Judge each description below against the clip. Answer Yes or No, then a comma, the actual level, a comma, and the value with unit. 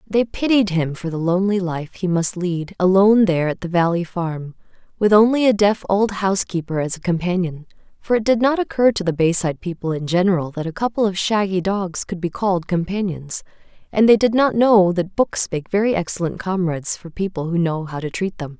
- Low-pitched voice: No, medium, 185 Hz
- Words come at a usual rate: No, fast, 210 wpm